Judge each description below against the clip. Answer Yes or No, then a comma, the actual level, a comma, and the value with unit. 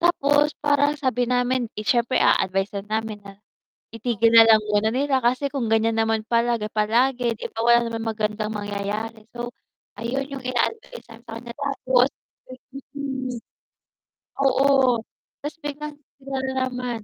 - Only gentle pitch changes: No, average, 3.3 semitones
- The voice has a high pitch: Yes, high, 240 Hz